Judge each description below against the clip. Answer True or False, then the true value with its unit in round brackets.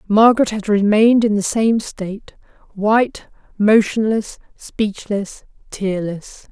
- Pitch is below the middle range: False (210 Hz)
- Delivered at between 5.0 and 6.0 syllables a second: False (4.0 syllables/s)